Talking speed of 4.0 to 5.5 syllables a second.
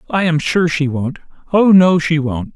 Yes: 4.5 syllables/s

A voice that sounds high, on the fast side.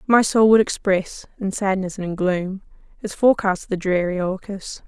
No: high, 195 Hz; average, 185 wpm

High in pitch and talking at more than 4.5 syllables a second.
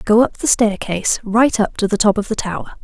Yes: high, 215 Hz; 5.6 syllables/s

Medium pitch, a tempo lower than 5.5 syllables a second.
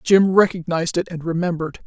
No: medium, 170 Hz; 6.3 syllables/s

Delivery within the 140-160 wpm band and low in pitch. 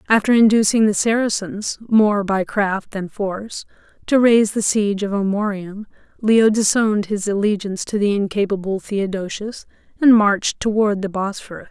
No: average, 145 wpm; high, 205 Hz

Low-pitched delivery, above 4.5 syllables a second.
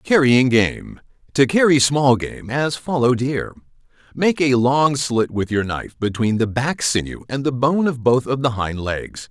No: low, 130 Hz; 4.4 syllables/s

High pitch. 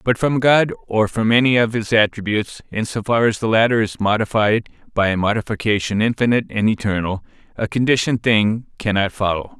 No: low, 110 Hz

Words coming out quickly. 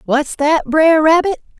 No: average, 150 wpm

